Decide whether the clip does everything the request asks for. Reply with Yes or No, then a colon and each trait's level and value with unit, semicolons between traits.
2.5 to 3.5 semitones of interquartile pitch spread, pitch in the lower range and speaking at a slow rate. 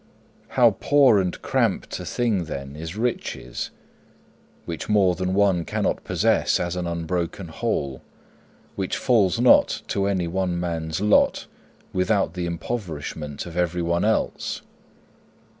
Yes: average, 3.1 semitones; very low, 90 Hz; slow, 125 wpm